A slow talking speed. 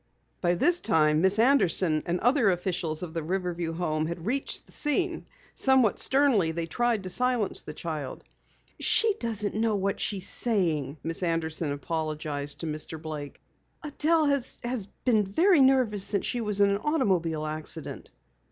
No: average, 160 wpm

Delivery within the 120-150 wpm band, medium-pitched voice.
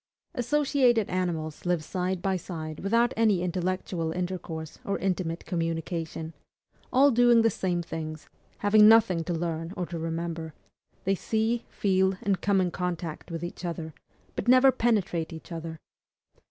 Yes: average, 145 wpm; medium, 180 Hz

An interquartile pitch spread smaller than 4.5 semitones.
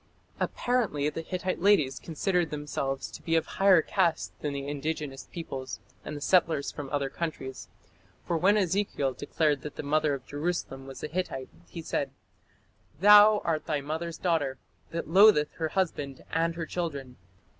Yes: average, 3.8 semitones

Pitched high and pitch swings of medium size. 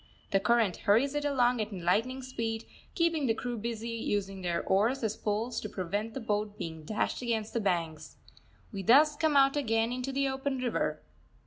Yes: high, 225 Hz; average, 4.1 semitones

